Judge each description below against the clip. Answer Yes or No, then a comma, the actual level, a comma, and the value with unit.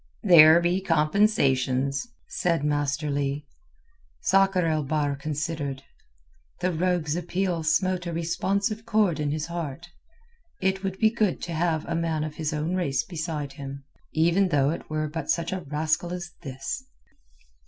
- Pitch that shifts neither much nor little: Yes, average, 3.3 semitones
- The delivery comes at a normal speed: Yes, average, 150 wpm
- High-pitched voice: No, medium, 165 Hz